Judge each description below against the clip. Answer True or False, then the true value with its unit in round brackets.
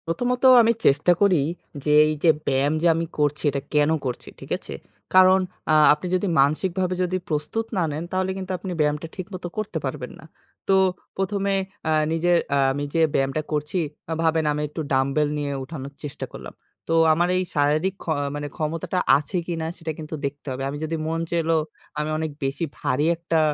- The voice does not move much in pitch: False (3.7 semitones)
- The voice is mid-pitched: True (160 Hz)